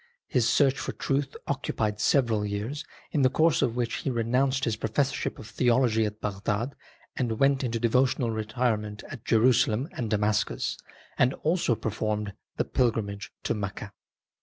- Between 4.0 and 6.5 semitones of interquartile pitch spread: No, average, 3.5 semitones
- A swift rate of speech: No, average, 150 wpm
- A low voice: Yes, low, 115 Hz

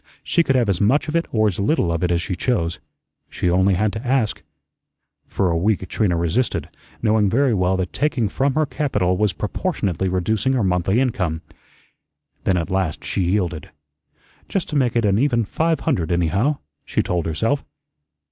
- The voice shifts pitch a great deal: Yes, wide, 6.2 semitones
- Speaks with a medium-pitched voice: No, low, 100 Hz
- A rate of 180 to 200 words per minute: Yes, average, 185 wpm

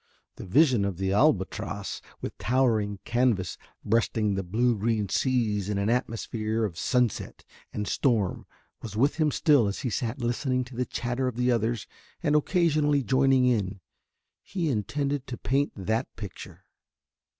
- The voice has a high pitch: No, low, 120 Hz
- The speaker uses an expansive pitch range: No, average, 4.0 semitones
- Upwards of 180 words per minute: No, average, 150 wpm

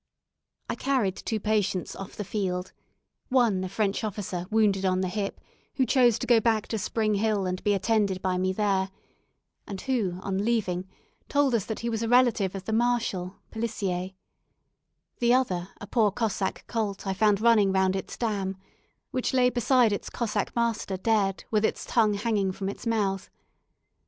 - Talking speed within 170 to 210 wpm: Yes, average, 175 wpm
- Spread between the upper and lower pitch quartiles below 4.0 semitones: Yes, average, 3.1 semitones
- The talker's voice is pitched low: No, high, 210 Hz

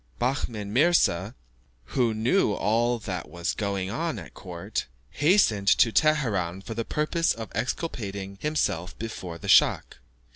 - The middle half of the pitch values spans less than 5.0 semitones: No, wide, 5.4 semitones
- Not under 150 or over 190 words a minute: No, slow, 135 wpm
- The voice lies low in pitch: Yes, low, 110 Hz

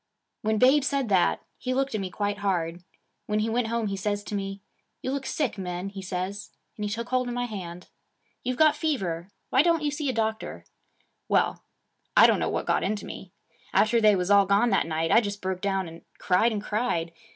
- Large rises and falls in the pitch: No, average, 4.2 semitones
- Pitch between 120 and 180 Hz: No, high, 205 Hz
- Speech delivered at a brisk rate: Yes, fast, 220 wpm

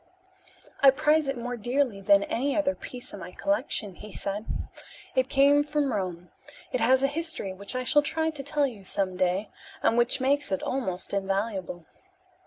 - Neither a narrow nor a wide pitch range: No, wide, 6.4 semitones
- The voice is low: No, high, 245 Hz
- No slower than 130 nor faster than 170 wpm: No, average, 180 wpm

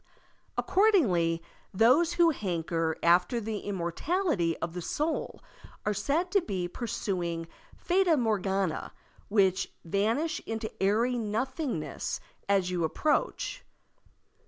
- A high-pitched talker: Yes, high, 210 Hz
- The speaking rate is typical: No, slow, 105 wpm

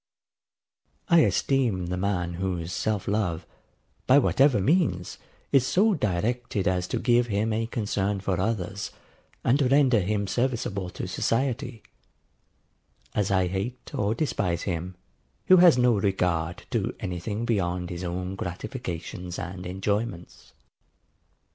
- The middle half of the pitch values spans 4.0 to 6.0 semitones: Yes, average, 4.9 semitones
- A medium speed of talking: No, slow, 130 wpm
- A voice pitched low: Yes, low, 100 Hz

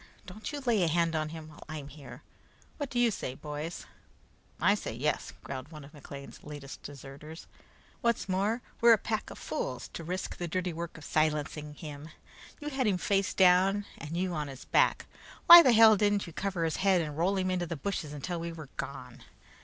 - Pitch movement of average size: Yes, average, 4.8 semitones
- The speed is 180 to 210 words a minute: Yes, fast, 205 wpm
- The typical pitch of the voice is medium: Yes, medium, 170 Hz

